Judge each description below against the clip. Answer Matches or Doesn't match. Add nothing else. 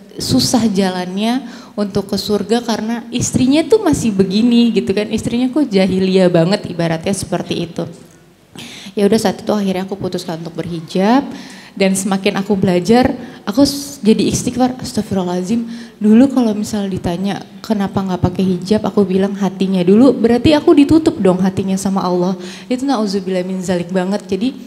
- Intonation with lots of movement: Doesn't match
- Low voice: Doesn't match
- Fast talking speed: Matches